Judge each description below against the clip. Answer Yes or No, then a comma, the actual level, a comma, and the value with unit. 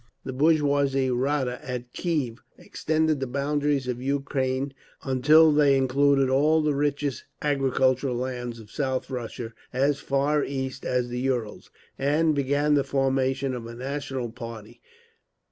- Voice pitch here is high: No, low, 135 Hz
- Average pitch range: No, narrow, 2.2 semitones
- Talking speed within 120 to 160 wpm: Yes, slow, 135 wpm